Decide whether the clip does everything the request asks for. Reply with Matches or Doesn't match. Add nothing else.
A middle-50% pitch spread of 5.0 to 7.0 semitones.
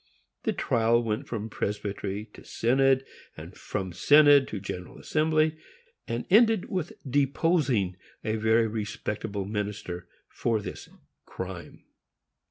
Matches